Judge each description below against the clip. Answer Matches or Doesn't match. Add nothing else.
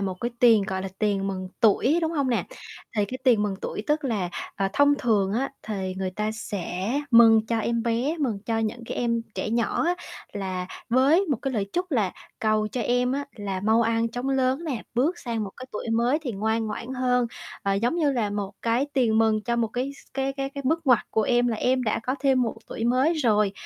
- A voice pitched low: Doesn't match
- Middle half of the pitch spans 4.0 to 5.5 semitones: Doesn't match